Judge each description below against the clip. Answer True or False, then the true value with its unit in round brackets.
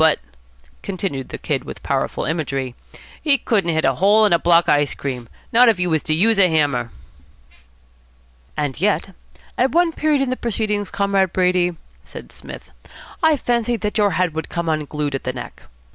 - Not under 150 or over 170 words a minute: False (185 wpm)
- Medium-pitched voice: True (180 Hz)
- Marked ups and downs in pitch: True (5.9 semitones)